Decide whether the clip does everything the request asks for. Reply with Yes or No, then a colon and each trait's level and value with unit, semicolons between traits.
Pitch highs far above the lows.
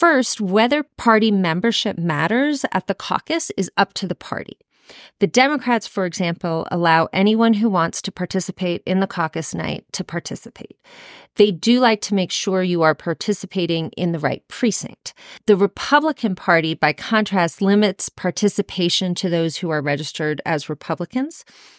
No: average, 5.0 semitones